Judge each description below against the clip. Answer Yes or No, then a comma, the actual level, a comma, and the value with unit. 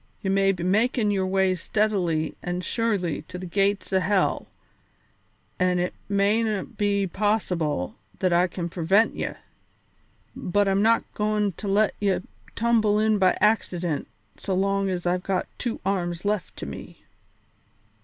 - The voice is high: Yes, high, 195 Hz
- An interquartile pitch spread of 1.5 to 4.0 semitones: Yes, narrow, 2.5 semitones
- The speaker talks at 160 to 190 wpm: No, average, 150 wpm